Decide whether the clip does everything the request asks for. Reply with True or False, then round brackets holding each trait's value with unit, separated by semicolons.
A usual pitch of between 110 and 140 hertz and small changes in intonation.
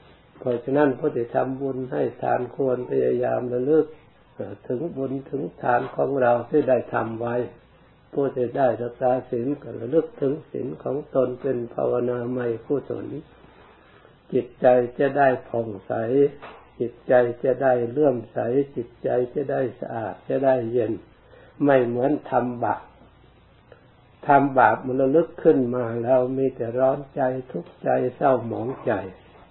True (125 Hz; 2.3 semitones)